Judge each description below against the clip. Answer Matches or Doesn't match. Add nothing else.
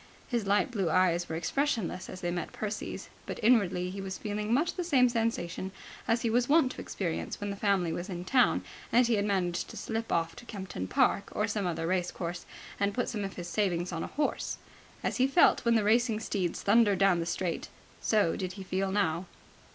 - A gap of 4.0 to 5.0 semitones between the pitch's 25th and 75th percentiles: Matches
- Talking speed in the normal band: Doesn't match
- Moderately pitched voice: Doesn't match